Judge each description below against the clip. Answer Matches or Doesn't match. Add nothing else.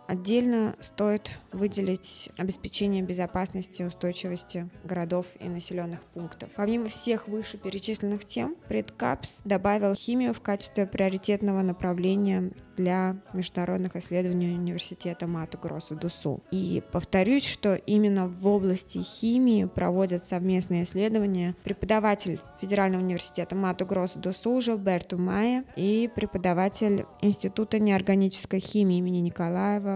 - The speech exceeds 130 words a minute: Doesn't match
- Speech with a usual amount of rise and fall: Doesn't match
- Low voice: Doesn't match